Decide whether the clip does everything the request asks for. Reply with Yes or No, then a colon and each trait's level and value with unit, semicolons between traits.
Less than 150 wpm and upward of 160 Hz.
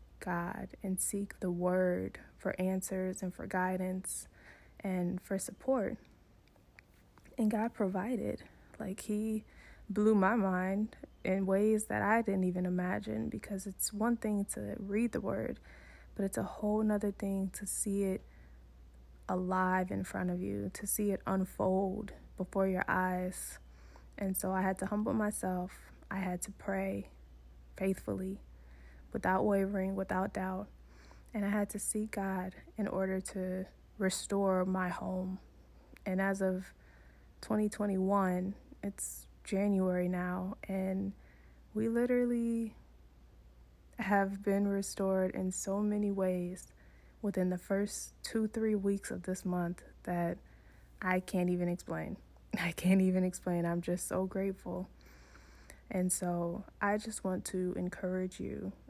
Yes: slow, 135 wpm; high, 190 Hz